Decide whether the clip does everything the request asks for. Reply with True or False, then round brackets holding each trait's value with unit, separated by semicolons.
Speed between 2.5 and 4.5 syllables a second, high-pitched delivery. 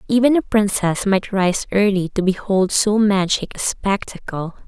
True (4.4 syllables/s; 200 Hz)